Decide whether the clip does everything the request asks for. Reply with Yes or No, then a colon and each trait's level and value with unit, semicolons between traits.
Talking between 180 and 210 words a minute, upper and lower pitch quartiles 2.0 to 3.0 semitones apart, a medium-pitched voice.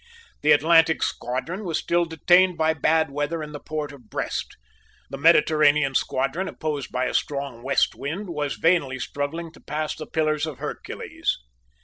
No: average, 160 wpm; narrow, 2.5 semitones; medium, 155 Hz